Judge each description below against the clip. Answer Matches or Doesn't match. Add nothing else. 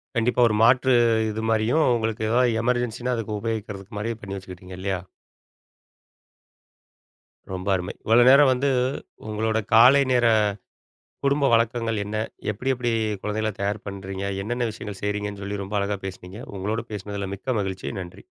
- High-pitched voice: Doesn't match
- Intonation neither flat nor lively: Matches